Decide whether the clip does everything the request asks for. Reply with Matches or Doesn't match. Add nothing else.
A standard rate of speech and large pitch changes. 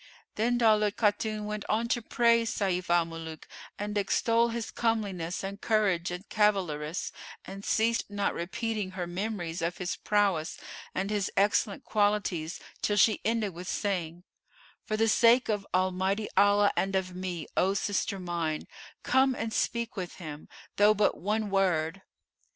Doesn't match